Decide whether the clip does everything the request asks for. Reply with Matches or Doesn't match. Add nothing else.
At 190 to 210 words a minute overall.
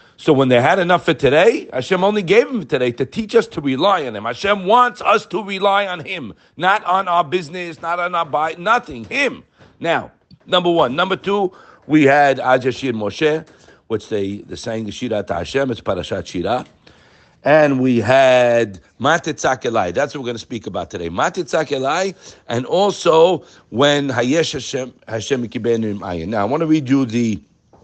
Doesn't match